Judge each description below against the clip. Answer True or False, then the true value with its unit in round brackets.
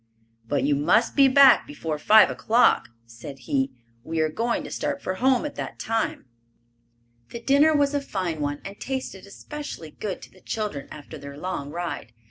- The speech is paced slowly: False (180 wpm)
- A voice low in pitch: False (185 Hz)